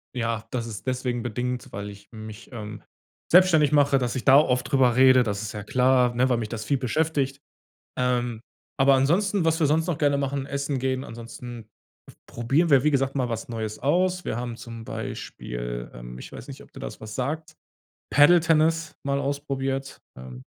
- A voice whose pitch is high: No, low, 130 Hz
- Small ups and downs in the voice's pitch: No, average, 3.6 semitones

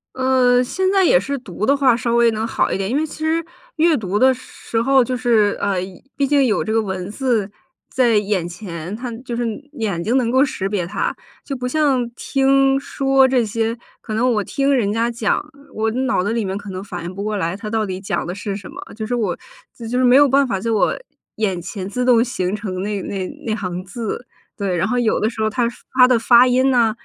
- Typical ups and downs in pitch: Yes, average, 4.2 semitones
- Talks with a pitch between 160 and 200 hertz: No, high, 230 Hz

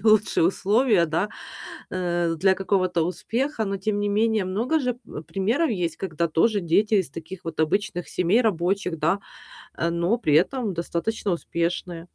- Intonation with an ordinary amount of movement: Yes, average, 4.0 semitones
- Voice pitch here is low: No, high, 190 Hz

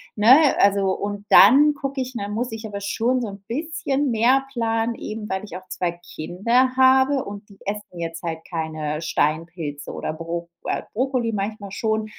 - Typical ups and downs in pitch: No, wide, 5.7 semitones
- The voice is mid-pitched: No, high, 210 Hz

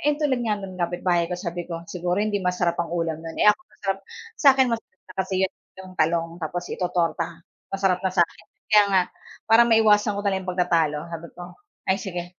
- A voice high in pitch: No, medium, 180 Hz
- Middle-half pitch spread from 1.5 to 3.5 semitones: Yes, average, 3.0 semitones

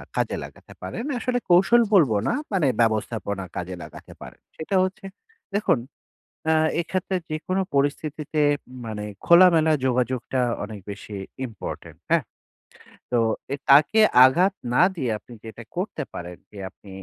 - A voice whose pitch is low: No, medium, 145 Hz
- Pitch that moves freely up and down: Yes, wide, 8.4 semitones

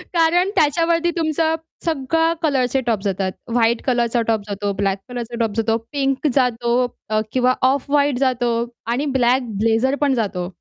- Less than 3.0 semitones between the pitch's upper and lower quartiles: No, average, 4.2 semitones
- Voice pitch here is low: No, very high, 250 Hz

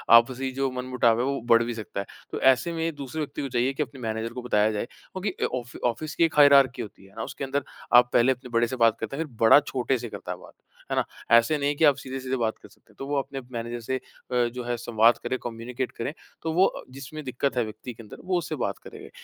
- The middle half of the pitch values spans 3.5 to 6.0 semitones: No, average, 2.9 semitones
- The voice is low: Yes, low, 125 Hz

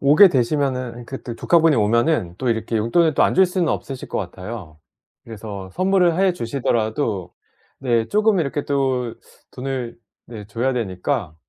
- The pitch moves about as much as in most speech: Yes, average, 5.0 semitones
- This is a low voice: Yes, low, 125 Hz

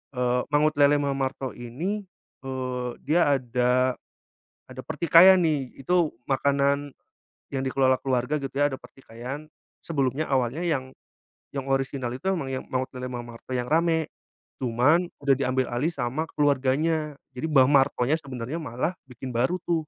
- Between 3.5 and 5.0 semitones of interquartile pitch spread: No, average, 3.1 semitones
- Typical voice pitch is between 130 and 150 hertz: Yes, low, 135 Hz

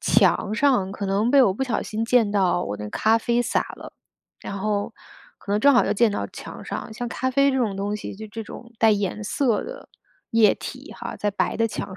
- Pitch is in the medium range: No, high, 220 Hz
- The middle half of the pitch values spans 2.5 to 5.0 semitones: Yes, average, 3.1 semitones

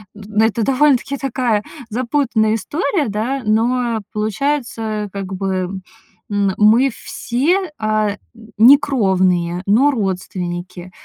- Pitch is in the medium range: No, high, 220 Hz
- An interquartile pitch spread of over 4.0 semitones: Yes, average, 4.5 semitones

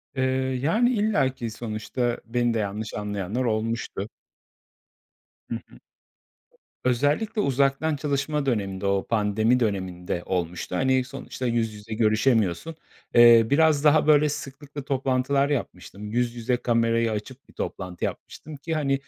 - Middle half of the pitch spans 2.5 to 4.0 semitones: No, average, 4.6 semitones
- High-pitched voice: No, low, 120 Hz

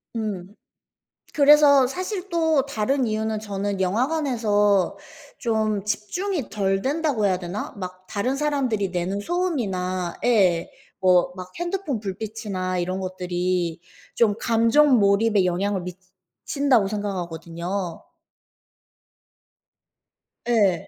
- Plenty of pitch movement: Yes, wide, 5.8 semitones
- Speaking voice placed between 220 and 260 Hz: No, high, 205 Hz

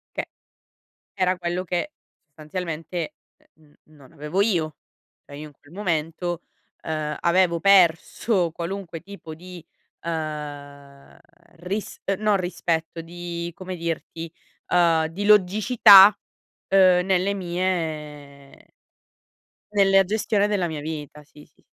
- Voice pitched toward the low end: No, medium, 170 Hz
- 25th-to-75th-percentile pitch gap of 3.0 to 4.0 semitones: Yes, average, 3.3 semitones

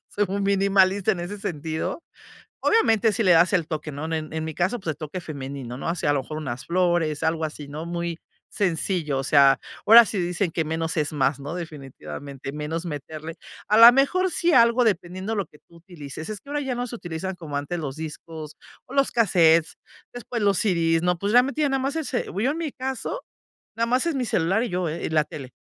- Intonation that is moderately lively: No, wide, 5.9 semitones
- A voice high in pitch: No, medium, 175 Hz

